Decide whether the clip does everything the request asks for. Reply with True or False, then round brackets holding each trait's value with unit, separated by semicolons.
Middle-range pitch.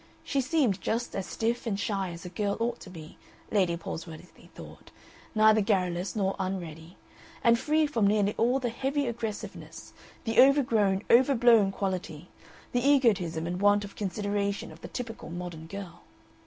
False (205 Hz)